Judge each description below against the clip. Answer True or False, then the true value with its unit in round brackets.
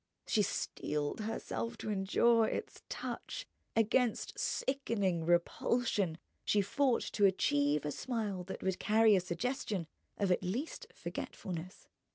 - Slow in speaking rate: True (125 wpm)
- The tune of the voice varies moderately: True (4.3 semitones)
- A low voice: False (200 Hz)